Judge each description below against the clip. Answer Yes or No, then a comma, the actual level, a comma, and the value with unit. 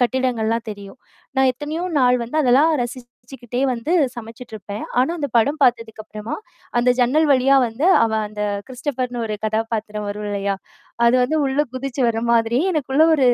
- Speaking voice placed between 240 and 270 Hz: Yes, high, 245 Hz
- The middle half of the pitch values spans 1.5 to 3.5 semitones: Yes, average, 3.2 semitones